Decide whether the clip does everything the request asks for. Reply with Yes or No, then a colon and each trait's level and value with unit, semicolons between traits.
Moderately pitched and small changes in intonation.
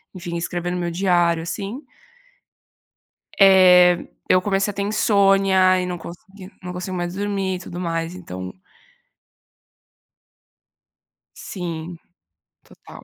Yes: medium, 180 Hz; narrow, 2.0 semitones